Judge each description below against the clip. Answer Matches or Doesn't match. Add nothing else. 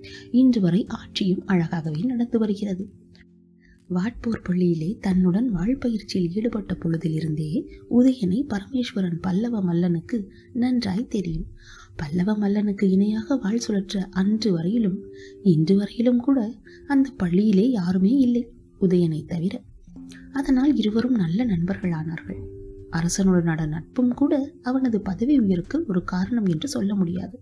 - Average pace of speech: Matches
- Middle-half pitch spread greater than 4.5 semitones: Matches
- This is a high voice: Matches